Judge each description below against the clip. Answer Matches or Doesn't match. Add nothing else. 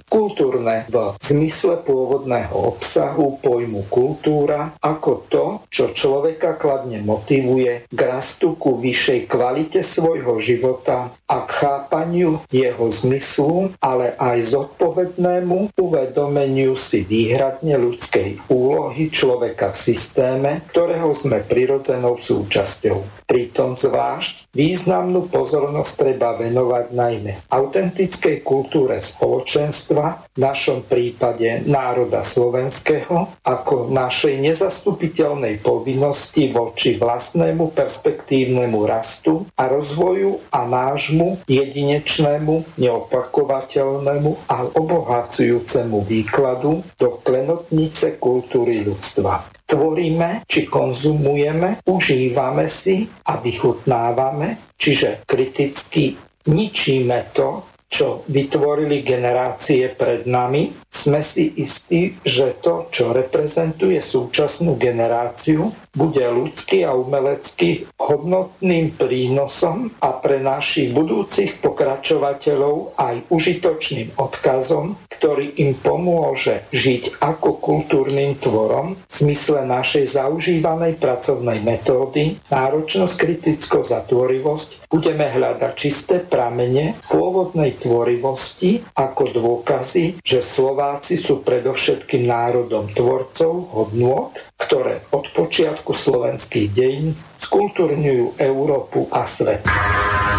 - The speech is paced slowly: Matches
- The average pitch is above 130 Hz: Matches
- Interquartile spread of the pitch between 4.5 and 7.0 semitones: Matches